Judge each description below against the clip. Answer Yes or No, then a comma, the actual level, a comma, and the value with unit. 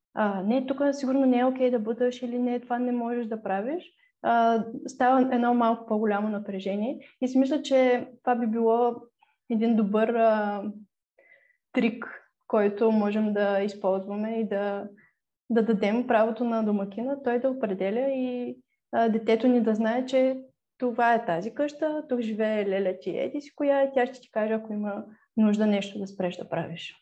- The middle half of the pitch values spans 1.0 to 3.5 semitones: Yes, average, 3.2 semitones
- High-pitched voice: Yes, high, 230 Hz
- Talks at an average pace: No, fast, 170 wpm